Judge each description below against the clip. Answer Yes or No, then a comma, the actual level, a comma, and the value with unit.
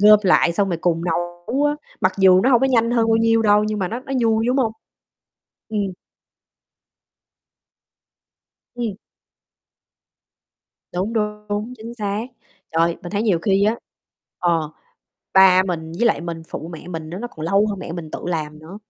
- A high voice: Yes, high, 200 Hz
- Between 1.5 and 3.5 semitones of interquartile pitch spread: No, average, 4.5 semitones